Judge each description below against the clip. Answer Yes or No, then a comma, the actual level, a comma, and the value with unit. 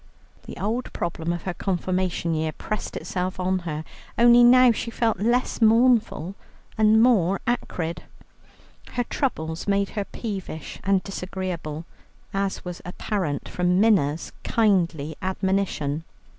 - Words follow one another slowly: Yes, slow, 125 wpm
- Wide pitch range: No, average, 4.4 semitones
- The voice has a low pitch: No, high, 190 Hz